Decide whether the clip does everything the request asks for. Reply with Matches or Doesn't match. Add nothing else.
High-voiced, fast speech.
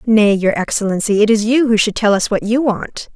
Matches